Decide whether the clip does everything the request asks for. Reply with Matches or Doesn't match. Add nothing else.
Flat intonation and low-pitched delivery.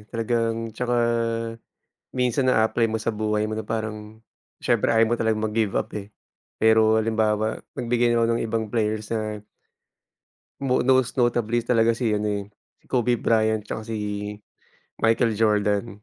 Matches